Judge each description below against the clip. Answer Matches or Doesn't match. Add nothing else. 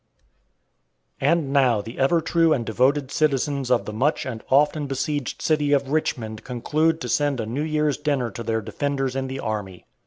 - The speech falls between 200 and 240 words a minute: Doesn't match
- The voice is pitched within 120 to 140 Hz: Matches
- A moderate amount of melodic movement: Matches